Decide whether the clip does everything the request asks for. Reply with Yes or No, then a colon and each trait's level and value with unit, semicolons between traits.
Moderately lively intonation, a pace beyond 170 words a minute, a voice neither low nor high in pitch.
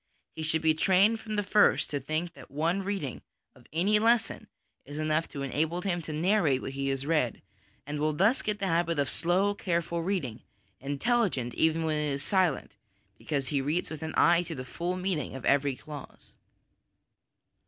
Yes: average, 4.5 semitones; average, 185 wpm; medium, 160 Hz